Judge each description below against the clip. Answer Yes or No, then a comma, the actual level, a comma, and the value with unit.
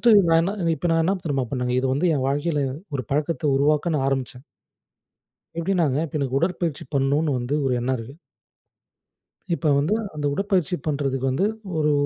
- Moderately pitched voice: Yes, medium, 145 Hz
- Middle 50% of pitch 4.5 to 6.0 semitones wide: No, average, 3.8 semitones